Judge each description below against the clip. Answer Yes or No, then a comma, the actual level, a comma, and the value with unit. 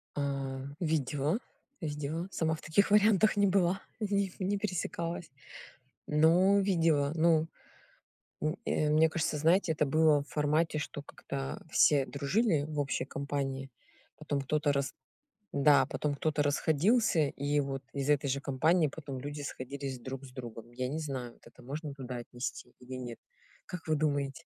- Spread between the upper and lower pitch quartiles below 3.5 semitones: Yes, average, 2.8 semitones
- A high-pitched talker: No, medium, 150 Hz